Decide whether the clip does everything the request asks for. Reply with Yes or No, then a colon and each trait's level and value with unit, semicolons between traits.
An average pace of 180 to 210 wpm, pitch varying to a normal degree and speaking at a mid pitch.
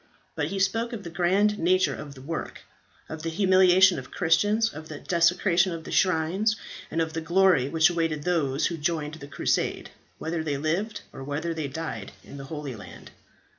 Yes: average, 190 wpm; average, 3.3 semitones; medium, 165 Hz